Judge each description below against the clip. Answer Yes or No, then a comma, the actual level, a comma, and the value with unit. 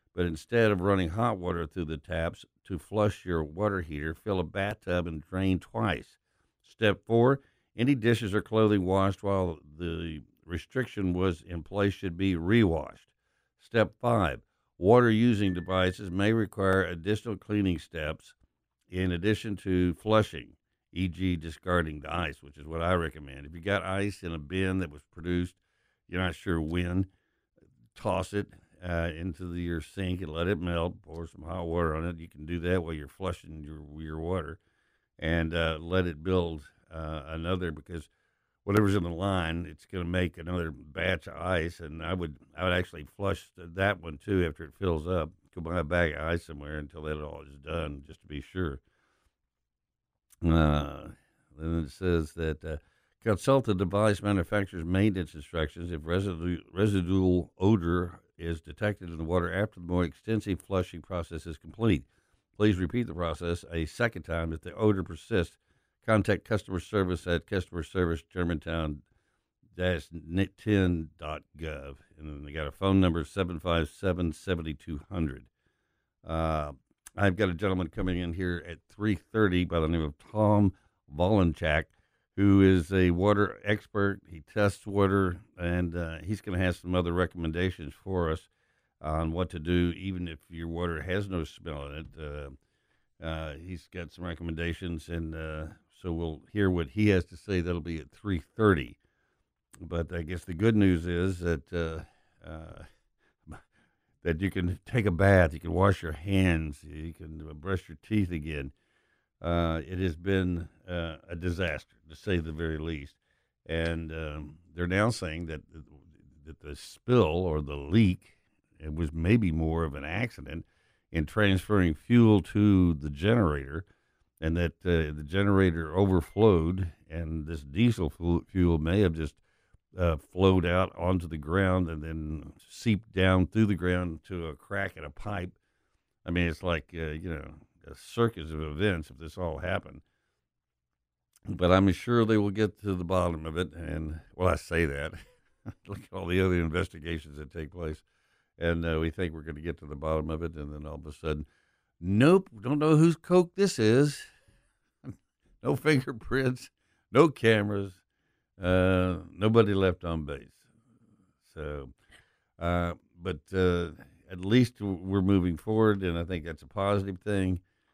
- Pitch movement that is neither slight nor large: Yes, average, 3.3 semitones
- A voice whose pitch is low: Yes, very low, 90 Hz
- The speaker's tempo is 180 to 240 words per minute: No, average, 165 wpm